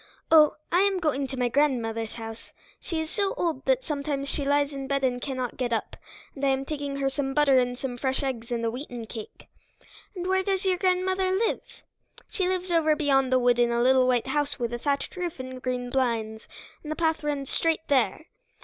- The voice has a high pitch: Yes, very high, 275 Hz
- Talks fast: Yes, fast, 215 wpm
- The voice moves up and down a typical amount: Yes, average, 4.3 semitones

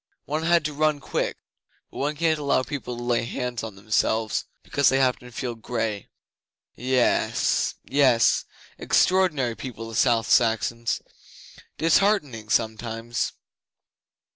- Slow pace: Yes, slow, 125 wpm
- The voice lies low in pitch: Yes, low, 125 Hz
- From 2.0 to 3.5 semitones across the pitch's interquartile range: No, average, 4.1 semitones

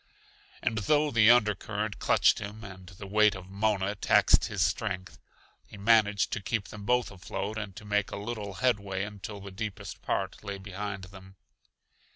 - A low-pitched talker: Yes, low, 105 Hz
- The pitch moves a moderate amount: No, narrow, 1.9 semitones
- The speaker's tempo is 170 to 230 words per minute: Yes, average, 175 wpm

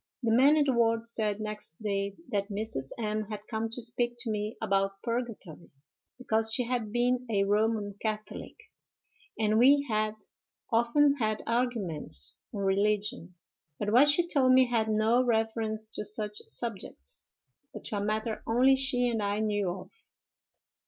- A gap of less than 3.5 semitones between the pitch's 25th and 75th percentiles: Yes, narrow, 2.5 semitones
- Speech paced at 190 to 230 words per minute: No, average, 160 wpm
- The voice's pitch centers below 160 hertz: No, high, 220 Hz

